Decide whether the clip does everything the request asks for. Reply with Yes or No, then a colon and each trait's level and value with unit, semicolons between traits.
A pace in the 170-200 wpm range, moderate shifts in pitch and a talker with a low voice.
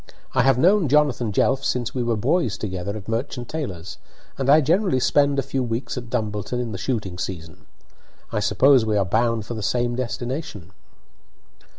Yes: average, 180 wpm; average, 4.3 semitones; low, 120 Hz